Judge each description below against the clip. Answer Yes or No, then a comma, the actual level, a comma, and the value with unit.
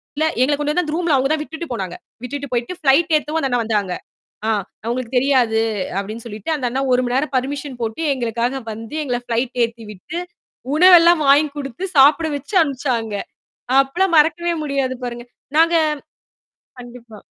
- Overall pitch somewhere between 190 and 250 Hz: No, very high, 270 Hz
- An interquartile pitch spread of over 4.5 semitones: No, average, 4.2 semitones